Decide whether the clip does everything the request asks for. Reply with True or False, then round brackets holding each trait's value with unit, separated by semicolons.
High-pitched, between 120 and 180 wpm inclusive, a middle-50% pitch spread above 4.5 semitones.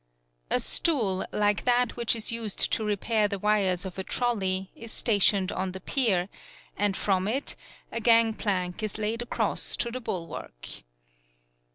False (210 Hz; 155 wpm; 3.4 semitones)